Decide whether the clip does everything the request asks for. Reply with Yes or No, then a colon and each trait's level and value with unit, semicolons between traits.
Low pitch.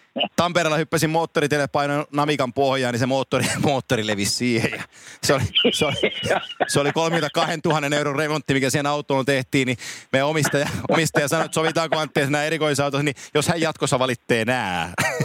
No: medium, 145 Hz